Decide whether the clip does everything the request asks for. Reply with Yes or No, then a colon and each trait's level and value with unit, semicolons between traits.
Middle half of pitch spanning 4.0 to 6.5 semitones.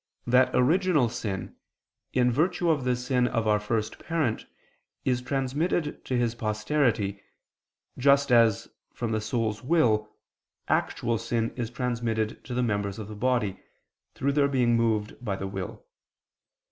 No: average, 3.3 semitones